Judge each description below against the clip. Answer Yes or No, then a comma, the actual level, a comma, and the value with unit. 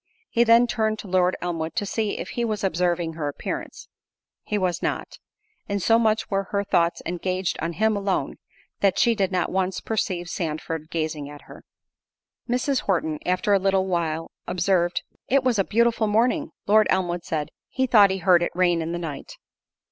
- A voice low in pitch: No, high, 190 Hz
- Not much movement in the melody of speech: No, average, 4.0 semitones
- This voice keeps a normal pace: Yes, average, 180 wpm